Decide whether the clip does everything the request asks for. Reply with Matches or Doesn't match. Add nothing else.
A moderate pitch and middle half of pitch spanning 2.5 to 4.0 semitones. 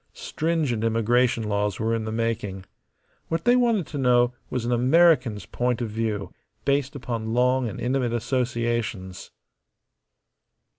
Doesn't match